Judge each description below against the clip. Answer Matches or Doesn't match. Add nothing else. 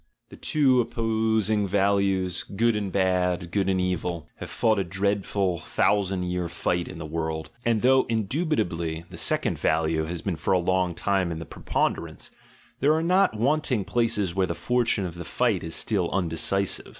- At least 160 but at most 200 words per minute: Matches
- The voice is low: Matches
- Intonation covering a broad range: Doesn't match